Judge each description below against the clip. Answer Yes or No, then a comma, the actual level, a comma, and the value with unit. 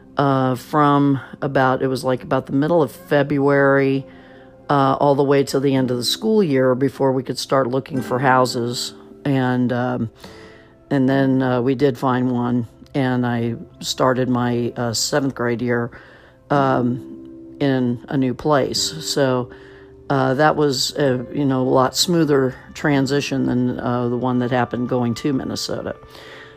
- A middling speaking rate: Yes, average, 160 wpm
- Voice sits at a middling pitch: No, low, 130 Hz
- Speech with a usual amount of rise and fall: No, narrow, 2.0 semitones